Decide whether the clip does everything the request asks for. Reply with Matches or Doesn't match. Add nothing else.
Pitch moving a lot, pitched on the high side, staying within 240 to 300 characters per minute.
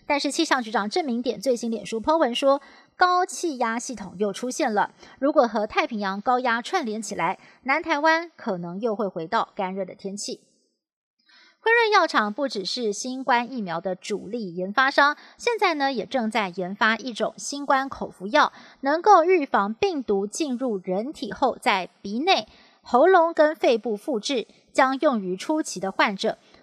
Matches